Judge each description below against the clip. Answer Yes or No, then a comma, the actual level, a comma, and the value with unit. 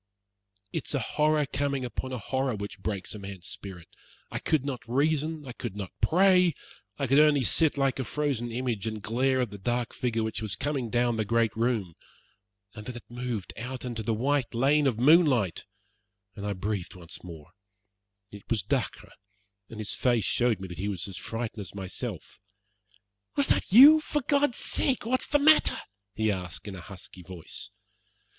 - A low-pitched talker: Yes, low, 120 Hz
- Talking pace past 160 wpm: Yes, average, 185 wpm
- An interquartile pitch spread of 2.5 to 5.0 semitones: No, wide, 5.4 semitones